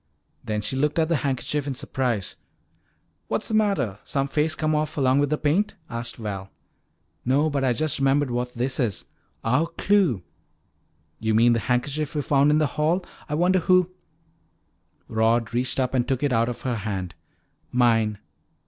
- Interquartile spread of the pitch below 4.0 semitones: No, average, 4.5 semitones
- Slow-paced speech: No, average, 175 wpm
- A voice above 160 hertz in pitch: No, low, 135 Hz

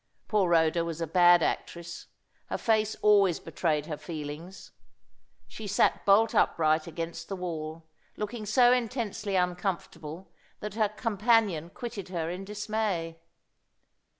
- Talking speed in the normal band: No, slow, 125 wpm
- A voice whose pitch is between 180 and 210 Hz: Yes, medium, 185 Hz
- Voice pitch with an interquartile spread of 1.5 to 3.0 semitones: No, average, 4.2 semitones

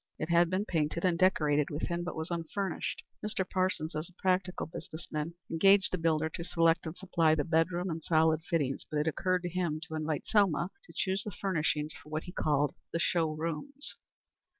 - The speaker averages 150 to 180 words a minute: No, average, 195 wpm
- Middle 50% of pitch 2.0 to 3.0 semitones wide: Yes, average, 2.7 semitones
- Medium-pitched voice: Yes, medium, 165 Hz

